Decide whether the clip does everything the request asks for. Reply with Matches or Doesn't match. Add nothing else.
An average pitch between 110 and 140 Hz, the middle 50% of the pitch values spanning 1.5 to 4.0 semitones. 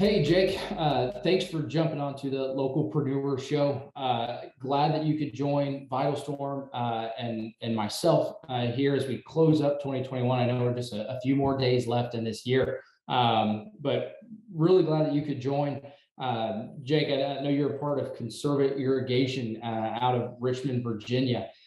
Matches